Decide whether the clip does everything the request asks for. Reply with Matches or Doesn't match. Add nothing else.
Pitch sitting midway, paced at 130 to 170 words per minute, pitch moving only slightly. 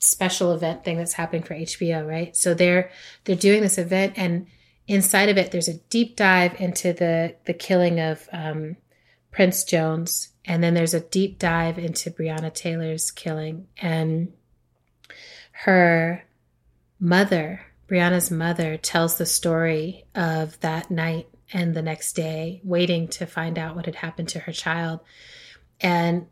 Matches